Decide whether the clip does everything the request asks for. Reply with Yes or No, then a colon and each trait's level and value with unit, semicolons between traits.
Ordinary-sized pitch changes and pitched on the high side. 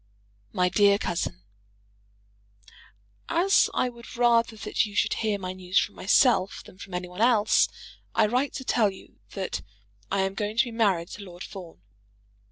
Yes: average, 4.0 semitones; high, 200 Hz